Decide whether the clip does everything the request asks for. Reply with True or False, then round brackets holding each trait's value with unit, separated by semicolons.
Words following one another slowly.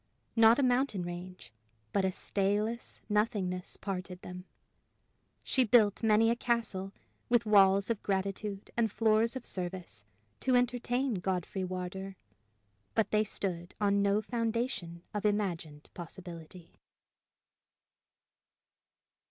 True (110 wpm)